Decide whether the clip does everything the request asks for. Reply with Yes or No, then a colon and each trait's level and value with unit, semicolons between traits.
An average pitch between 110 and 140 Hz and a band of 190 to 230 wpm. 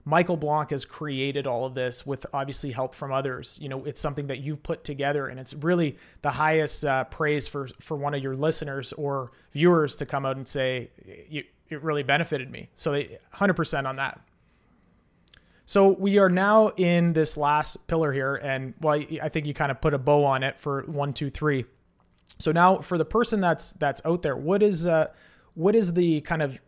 No: medium, 150 Hz; fast, 205 wpm